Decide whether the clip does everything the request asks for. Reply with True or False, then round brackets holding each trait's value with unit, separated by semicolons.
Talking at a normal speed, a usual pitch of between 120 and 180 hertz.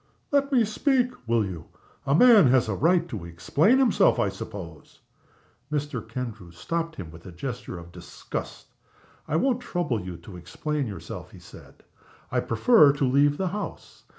True (170 wpm; 135 Hz)